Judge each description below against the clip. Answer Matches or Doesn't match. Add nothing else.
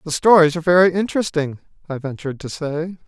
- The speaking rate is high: Doesn't match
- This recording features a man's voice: Matches